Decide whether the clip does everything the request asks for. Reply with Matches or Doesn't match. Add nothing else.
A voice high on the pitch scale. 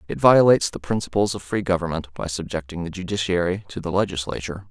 Doesn't match